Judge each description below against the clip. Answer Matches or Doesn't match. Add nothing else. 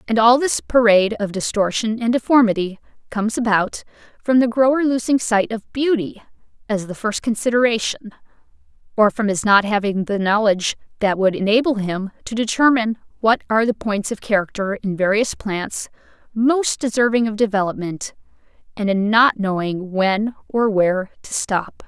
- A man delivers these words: Doesn't match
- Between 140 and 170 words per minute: Matches